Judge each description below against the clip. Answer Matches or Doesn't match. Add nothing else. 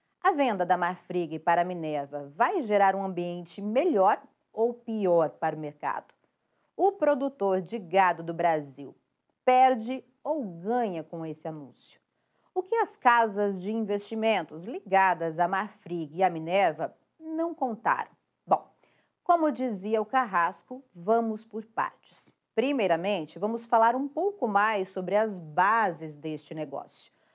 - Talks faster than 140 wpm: Doesn't match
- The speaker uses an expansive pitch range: Matches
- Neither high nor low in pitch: Doesn't match